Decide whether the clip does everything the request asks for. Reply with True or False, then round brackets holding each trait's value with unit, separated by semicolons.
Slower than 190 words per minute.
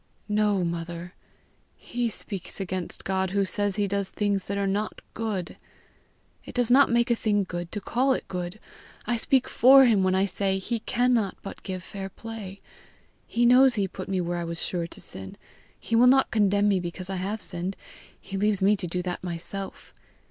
False (195 wpm)